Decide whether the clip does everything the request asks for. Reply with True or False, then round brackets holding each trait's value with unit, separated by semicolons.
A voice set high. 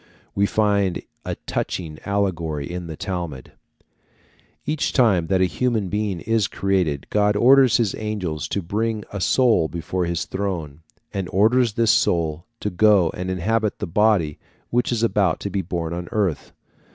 False (95 Hz)